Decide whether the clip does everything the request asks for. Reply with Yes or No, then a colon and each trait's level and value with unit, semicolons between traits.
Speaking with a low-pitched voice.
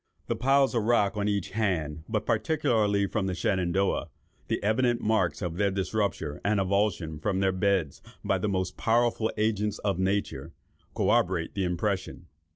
Yes: low, 100 Hz